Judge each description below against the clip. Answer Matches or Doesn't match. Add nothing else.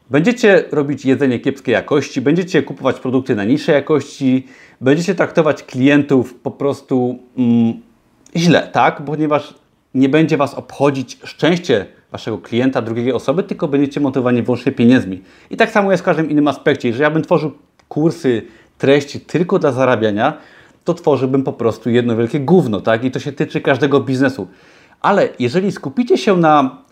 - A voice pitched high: Doesn't match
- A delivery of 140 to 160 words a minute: Matches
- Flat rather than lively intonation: Doesn't match